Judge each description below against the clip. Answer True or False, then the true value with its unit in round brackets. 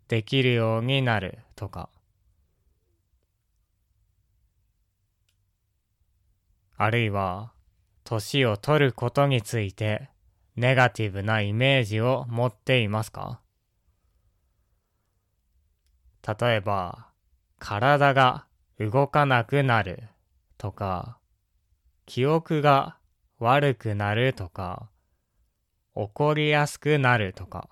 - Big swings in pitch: False (5.0 semitones)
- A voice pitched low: True (105 Hz)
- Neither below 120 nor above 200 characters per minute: True (160 characters per minute)